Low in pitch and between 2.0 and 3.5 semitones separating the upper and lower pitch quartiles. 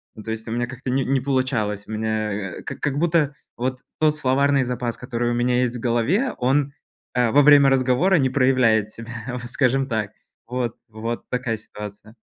Yes: low, 125 Hz; average, 2.9 semitones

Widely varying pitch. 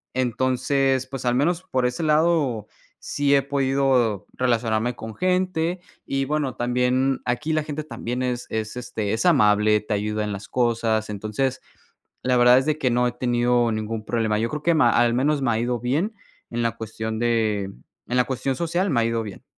No: average, 3.3 semitones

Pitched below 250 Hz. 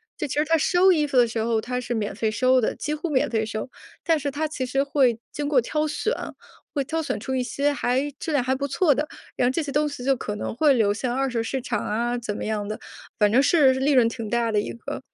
No: very high, 260 Hz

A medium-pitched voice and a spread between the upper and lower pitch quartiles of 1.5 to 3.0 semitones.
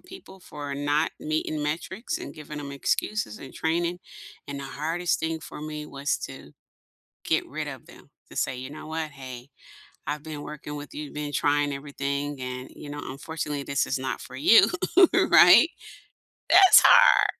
Yes: medium, 150 Hz; narrow, 2.4 semitones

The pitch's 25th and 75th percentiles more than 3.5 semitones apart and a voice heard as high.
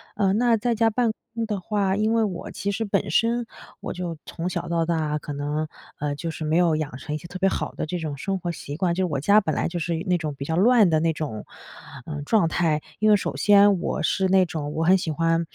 No: average, 4.4 semitones; medium, 175 Hz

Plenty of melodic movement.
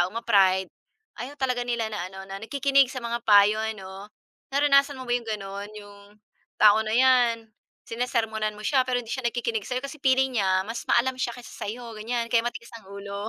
No: average, 3.4 semitones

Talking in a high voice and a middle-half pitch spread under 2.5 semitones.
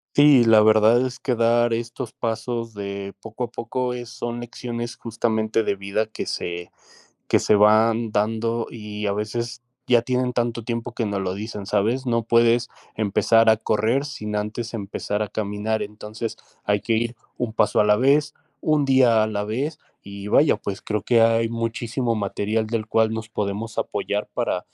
No: low, 115 Hz; narrow, 2.0 semitones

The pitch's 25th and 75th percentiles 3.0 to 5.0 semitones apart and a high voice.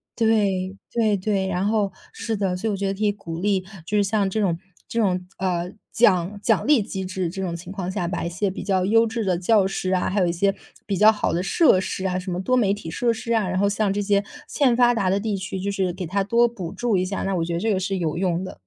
No: narrow, 2.5 semitones; high, 195 Hz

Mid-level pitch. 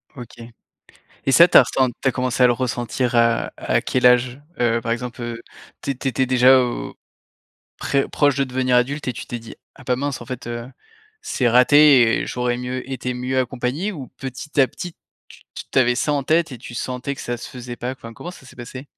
No: low, 125 Hz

